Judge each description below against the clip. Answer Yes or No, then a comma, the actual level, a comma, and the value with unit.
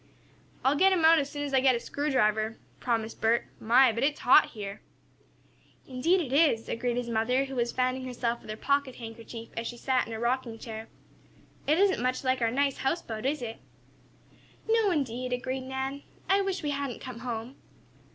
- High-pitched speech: Yes, very high, 255 Hz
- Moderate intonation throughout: Yes, average, 3.3 semitones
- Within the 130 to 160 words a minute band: No, average, 190 wpm